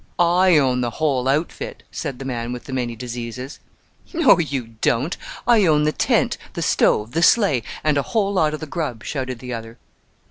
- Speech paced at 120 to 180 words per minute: No, average, 190 wpm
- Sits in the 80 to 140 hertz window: Yes, low, 135 Hz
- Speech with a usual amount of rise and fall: Yes, average, 4.7 semitones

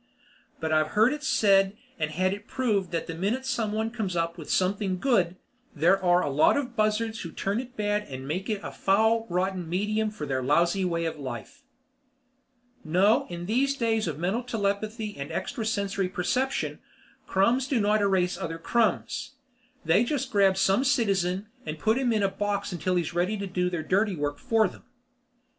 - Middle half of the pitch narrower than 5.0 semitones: Yes, average, 4.0 semitones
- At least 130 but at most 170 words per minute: No, average, 190 wpm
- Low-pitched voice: No, high, 195 Hz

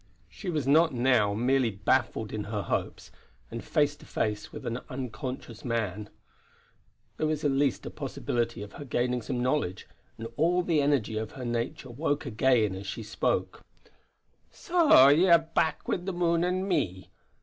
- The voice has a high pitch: No, low, 130 Hz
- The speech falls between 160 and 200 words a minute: Yes, average, 170 wpm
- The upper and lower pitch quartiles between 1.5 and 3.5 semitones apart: No, wide, 5.6 semitones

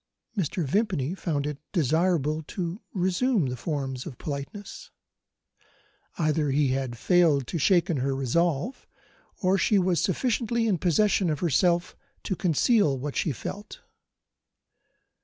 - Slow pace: Yes, slow, 125 wpm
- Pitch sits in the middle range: Yes, medium, 170 Hz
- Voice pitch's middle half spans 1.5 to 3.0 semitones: No, average, 5.0 semitones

